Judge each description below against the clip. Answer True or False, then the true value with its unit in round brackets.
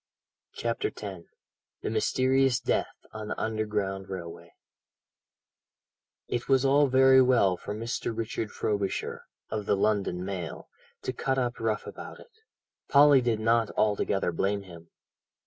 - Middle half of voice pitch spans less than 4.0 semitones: False (4.8 semitones)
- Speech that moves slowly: True (130 wpm)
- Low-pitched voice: True (110 Hz)